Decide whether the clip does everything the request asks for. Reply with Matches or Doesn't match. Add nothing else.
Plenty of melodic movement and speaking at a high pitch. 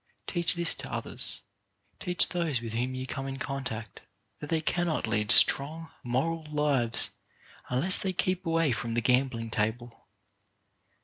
Doesn't match